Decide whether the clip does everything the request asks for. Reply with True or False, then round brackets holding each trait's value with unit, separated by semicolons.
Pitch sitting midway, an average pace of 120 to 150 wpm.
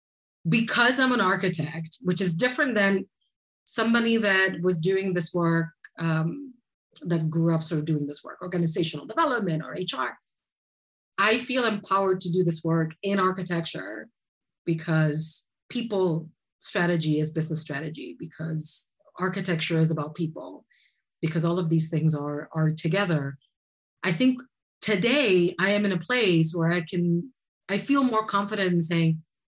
True (175 Hz; 145 wpm)